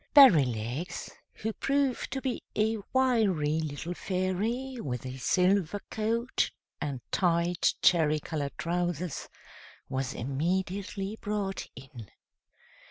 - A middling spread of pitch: No, wide, 6.5 semitones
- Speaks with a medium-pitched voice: Yes, medium, 180 Hz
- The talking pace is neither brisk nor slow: No, slow, 100 wpm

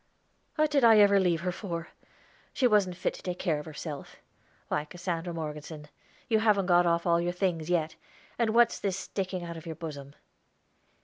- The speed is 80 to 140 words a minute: No, average, 185 wpm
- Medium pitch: Yes, medium, 175 Hz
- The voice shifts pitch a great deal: No, average, 3.3 semitones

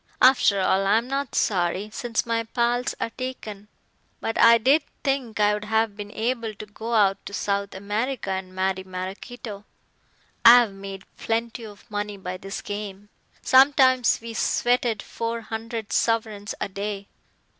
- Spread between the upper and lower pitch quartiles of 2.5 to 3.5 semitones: Yes, average, 2.8 semitones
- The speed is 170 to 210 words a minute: No, average, 145 wpm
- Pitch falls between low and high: No, high, 220 Hz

